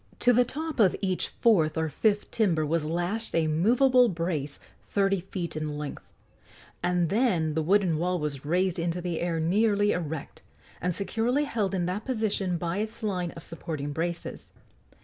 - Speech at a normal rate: Yes, average, 170 wpm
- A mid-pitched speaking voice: Yes, medium, 180 Hz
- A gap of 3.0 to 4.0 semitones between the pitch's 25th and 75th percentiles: No, average, 4.4 semitones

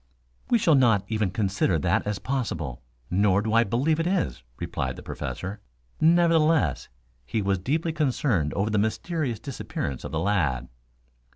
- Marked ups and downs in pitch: Yes, wide, 8.3 semitones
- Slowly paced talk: No, average, 155 wpm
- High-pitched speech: No, low, 110 Hz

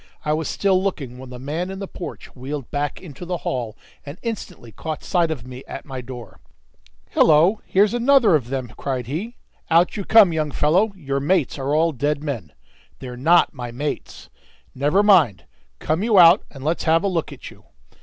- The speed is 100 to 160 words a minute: No, average, 195 wpm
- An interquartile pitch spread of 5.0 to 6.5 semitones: Yes, wide, 5.6 semitones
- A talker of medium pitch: Yes, medium, 155 Hz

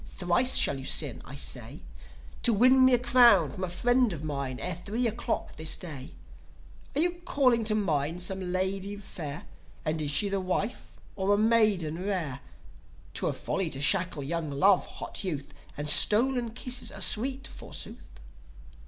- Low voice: No, high, 190 Hz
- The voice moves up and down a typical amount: No, wide, 6.7 semitones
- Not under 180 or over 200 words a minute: No, average, 170 wpm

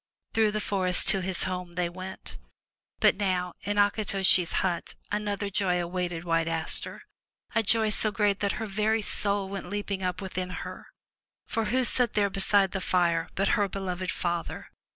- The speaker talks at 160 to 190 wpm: Yes, average, 170 wpm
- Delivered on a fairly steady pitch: Yes, narrow, 2.3 semitones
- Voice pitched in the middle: No, high, 195 Hz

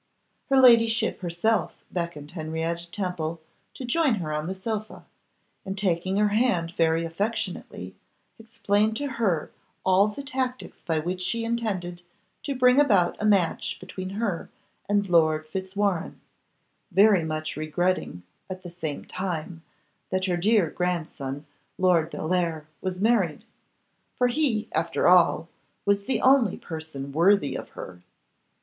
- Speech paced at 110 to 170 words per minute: Yes, slow, 135 wpm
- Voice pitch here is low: No, medium, 185 Hz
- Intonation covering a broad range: No, average, 4.6 semitones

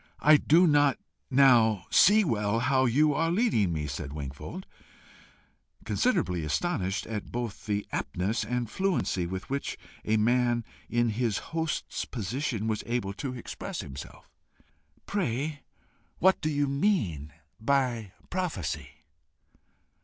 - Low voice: Yes, low, 120 Hz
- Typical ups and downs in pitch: No, wide, 6.5 semitones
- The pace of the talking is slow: Yes, slow, 125 wpm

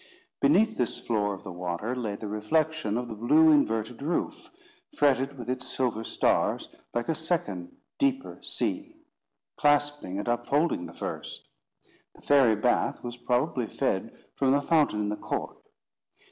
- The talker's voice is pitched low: Yes, low, 125 Hz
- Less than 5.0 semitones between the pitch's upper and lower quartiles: No, wide, 5.6 semitones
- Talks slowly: No, average, 150 wpm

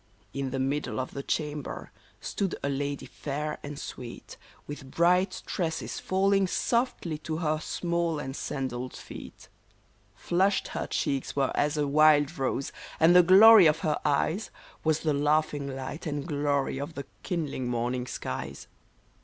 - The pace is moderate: Yes, average, 150 wpm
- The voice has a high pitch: No, medium, 150 Hz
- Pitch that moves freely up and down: No, average, 3.4 semitones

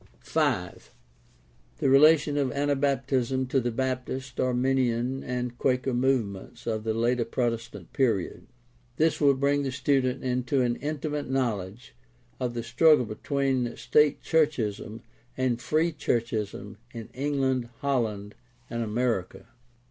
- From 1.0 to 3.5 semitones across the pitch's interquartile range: Yes, average, 2.8 semitones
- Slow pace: Yes, slow, 125 wpm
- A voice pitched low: Yes, low, 125 Hz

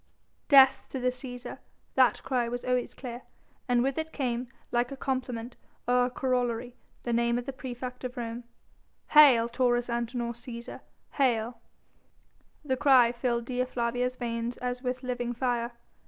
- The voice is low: No, high, 245 Hz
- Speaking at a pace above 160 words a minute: No, average, 155 wpm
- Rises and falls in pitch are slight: Yes, narrow, 1.2 semitones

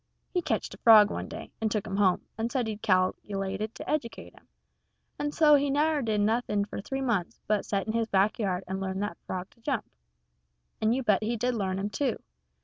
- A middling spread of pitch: Yes, average, 3.8 semitones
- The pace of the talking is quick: Yes, fast, 225 wpm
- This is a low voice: No, high, 215 Hz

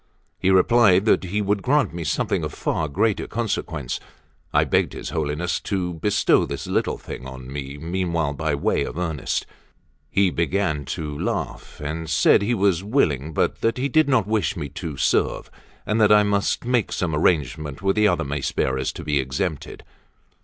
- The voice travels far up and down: Yes, wide, 5.7 semitones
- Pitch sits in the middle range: No, very low, 85 Hz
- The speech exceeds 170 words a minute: Yes, average, 180 wpm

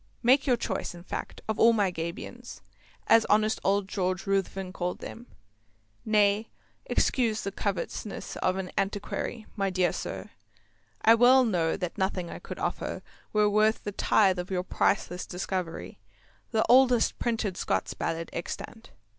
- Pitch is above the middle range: Yes, high, 200 Hz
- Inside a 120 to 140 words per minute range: No, average, 150 wpm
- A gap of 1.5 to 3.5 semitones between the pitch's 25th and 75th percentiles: Yes, average, 3.2 semitones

